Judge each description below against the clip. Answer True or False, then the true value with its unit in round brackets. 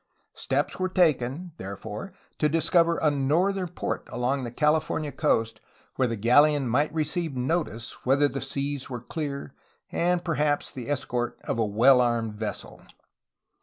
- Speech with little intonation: False (4.5 semitones)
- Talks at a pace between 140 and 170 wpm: True (150 wpm)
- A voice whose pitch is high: False (140 Hz)